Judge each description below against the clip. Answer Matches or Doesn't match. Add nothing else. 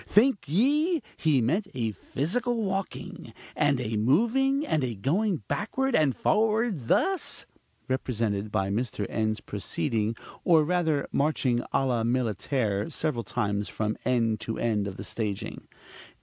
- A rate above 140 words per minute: Doesn't match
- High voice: Doesn't match